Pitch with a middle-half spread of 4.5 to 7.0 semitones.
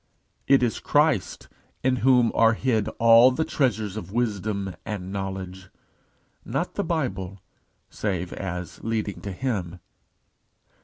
No: average, 3.6 semitones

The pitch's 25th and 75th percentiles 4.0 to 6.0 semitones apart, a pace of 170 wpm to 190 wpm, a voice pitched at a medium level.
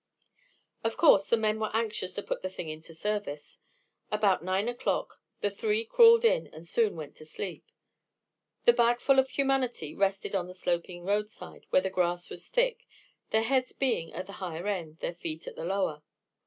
No: average, 5.0 semitones; average, 180 wpm; high, 200 Hz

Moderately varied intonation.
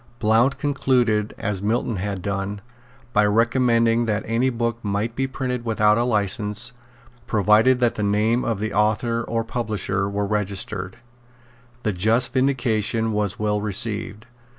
No: narrow, 2.3 semitones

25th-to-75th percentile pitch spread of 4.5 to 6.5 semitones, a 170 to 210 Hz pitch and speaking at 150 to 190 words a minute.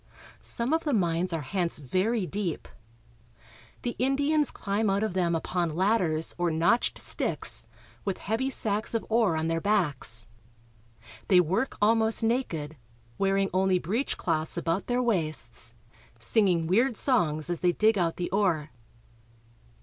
No: average, 5.2 semitones; high, 190 Hz; average, 140 wpm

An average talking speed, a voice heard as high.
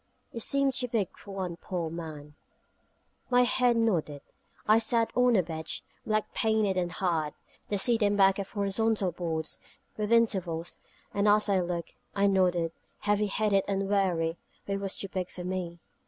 Yes: average, 170 wpm; high, 195 Hz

